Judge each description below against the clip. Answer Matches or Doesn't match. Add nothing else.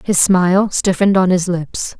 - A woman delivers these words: Matches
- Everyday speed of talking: Matches